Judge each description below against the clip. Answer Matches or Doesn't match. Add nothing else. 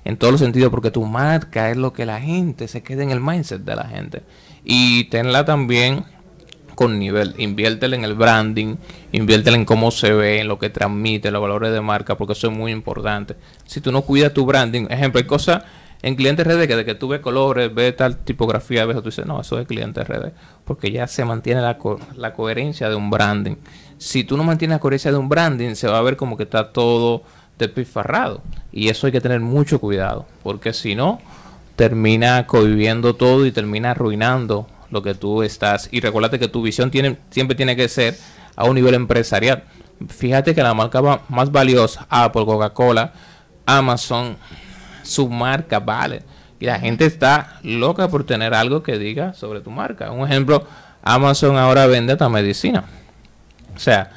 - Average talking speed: Doesn't match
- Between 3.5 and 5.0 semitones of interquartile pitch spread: Matches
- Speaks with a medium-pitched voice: Doesn't match